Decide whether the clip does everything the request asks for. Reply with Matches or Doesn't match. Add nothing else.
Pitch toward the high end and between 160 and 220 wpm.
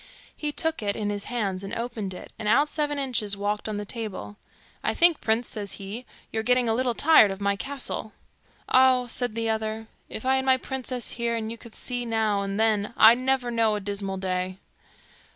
Matches